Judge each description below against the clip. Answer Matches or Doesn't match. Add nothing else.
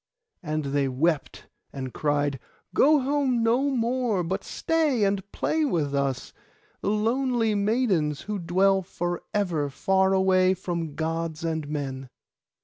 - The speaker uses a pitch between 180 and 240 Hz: Matches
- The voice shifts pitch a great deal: Matches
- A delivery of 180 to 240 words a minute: Doesn't match